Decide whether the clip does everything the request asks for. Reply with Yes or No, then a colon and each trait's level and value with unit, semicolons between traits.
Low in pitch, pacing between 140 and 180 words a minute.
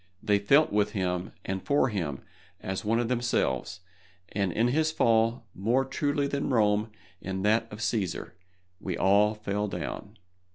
Yes: low, 105 Hz; average, 155 wpm